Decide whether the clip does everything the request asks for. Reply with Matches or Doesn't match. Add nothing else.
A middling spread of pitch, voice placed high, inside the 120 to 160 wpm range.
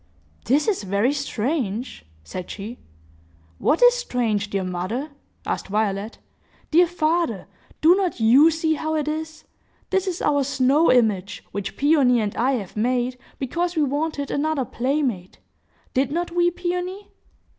Doesn't match